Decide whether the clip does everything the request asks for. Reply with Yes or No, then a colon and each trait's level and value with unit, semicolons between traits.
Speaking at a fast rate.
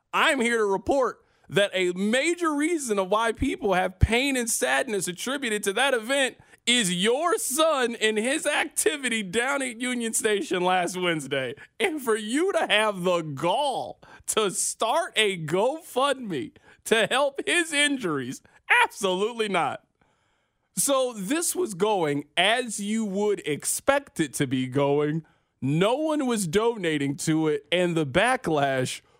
No: average, 140 wpm